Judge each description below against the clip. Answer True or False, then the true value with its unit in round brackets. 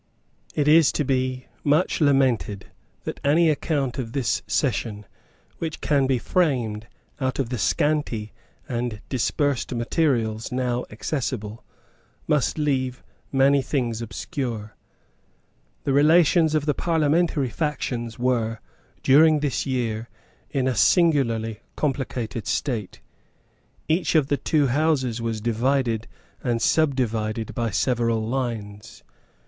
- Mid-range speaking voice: False (130 Hz)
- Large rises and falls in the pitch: False (4.2 semitones)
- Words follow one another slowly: True (115 wpm)